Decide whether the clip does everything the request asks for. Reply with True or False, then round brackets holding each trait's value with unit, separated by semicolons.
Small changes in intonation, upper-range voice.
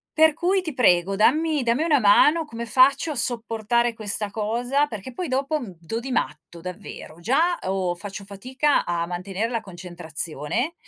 False (6.5 semitones; 230 Hz)